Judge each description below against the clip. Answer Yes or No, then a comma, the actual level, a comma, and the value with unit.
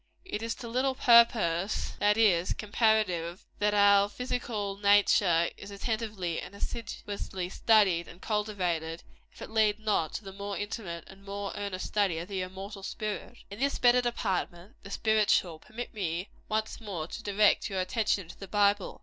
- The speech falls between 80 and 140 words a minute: No, average, 165 wpm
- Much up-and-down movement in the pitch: No, average, 2.8 semitones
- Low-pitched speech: No, high, 205 Hz